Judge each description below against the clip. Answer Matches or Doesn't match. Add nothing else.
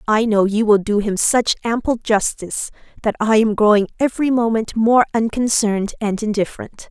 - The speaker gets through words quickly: Doesn't match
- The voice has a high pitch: Matches